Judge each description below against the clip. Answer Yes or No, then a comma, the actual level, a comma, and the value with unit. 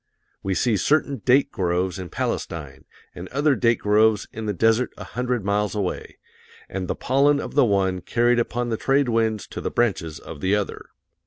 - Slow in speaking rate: No, average, 185 wpm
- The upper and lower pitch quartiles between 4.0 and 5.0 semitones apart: Yes, average, 4.5 semitones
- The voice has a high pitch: No, low, 110 Hz